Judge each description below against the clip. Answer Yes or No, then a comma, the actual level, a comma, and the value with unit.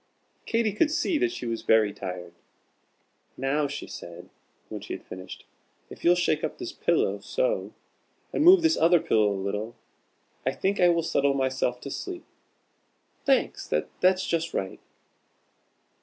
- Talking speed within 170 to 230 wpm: No, average, 155 wpm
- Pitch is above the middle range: No, medium, 160 Hz